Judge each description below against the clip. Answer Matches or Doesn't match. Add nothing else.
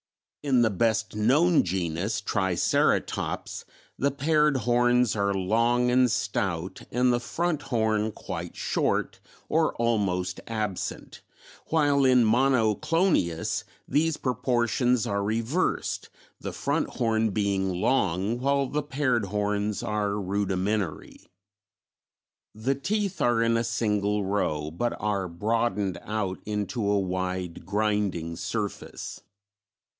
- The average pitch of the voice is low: Matches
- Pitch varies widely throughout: Doesn't match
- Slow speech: Matches